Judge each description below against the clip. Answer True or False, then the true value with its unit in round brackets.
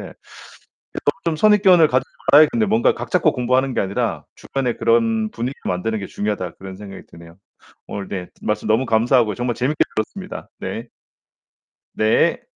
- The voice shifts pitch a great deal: True (5.9 semitones)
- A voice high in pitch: False (120 Hz)